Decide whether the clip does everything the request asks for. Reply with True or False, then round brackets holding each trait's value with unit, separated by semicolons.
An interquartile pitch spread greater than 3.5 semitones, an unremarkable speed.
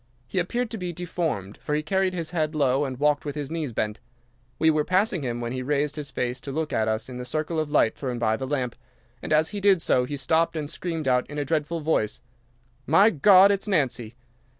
False (4.6 semitones; 235 wpm)